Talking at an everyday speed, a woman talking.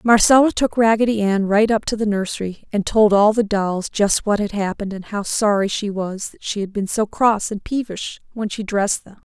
No: fast, 225 wpm; female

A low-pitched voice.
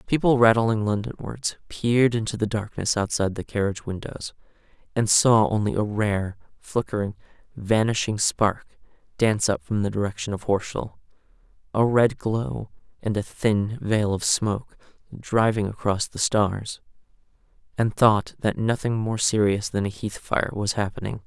Yes: low, 105 Hz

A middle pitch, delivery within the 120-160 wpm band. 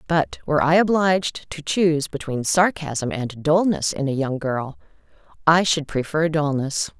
Yes: medium, 150 Hz; average, 155 wpm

